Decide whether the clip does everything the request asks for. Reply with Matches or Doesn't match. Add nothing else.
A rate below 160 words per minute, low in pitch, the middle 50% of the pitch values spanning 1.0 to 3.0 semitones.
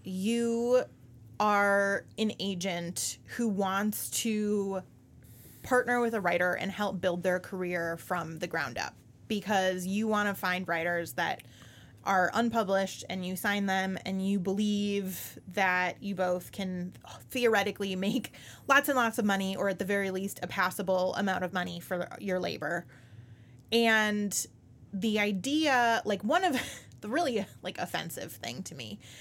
Doesn't match